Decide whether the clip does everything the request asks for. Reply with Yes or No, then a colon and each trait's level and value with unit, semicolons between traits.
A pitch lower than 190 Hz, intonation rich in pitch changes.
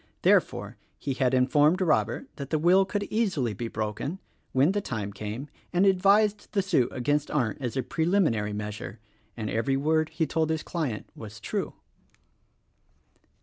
Yes: medium, 140 Hz; wide, 7.4 semitones